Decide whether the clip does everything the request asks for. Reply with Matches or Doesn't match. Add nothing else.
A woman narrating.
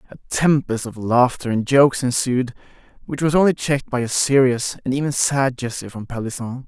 Doesn't match